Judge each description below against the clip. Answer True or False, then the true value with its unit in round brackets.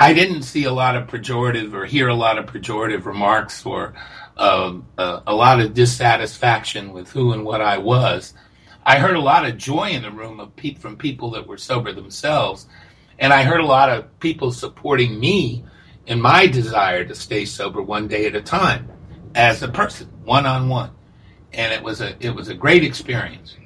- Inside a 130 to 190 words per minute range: False (200 wpm)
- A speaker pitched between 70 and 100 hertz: False (120 Hz)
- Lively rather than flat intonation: False (3.6 semitones)